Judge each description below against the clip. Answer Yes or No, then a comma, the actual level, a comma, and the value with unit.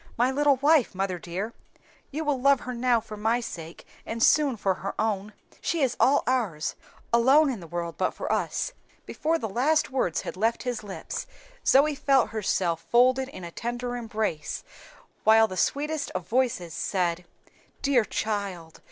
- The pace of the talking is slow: No, average, 170 wpm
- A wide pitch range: Yes, wide, 5.7 semitones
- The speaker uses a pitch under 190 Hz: No, high, 230 Hz